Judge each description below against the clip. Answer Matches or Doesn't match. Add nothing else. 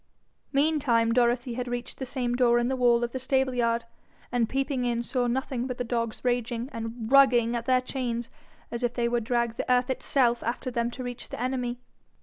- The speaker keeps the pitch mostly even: Matches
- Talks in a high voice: Matches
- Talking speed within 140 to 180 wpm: Doesn't match